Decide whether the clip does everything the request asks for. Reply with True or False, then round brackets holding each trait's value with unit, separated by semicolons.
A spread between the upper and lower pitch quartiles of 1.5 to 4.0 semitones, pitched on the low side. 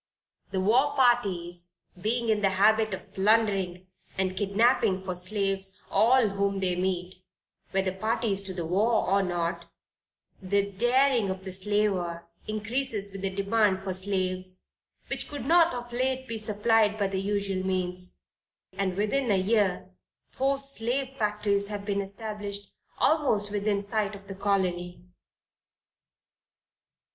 False (2.7 semitones; 200 Hz)